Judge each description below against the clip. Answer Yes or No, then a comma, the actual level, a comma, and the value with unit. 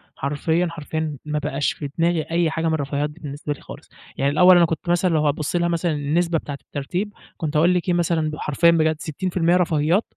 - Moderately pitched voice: Yes, medium, 160 Hz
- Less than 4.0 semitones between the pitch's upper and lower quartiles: Yes, narrow, 2.5 semitones